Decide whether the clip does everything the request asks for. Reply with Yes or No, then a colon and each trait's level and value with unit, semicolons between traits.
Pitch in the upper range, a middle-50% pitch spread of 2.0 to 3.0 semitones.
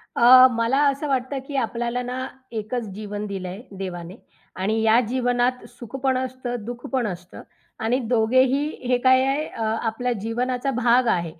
Yes: high, 245 Hz; average, 2.7 semitones